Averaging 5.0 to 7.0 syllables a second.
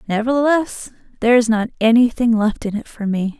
Yes: 5.6 syllables/s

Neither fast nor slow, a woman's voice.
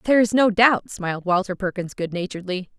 Yes: average, 195 wpm; female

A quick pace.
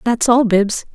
No: average, 190 wpm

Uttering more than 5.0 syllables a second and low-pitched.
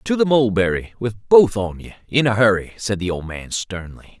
No: 4.9 syllables/s; low, 110 Hz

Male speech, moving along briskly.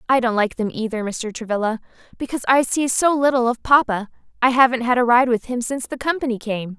No: female; fast, 220 wpm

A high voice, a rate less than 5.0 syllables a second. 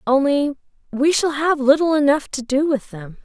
Yes: very high, 280 Hz; 4.8 syllables/s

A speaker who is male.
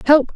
Yes: male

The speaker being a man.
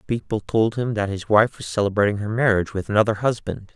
Yes: male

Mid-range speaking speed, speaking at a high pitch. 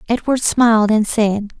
Yes: average, 150 wpm; high, 220 Hz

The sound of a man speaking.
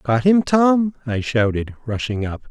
Yes: male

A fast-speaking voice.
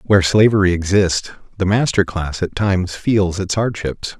No: average, 155 wpm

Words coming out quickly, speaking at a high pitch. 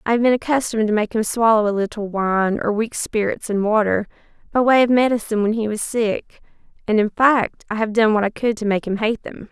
Yes: fast, 240 wpm; high, 220 Hz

